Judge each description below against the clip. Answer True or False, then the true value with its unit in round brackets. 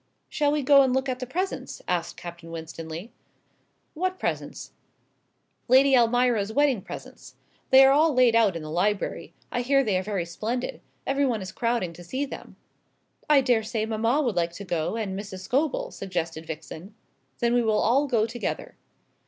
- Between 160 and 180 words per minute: True (170 wpm)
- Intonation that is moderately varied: False (6.2 semitones)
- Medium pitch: False (230 Hz)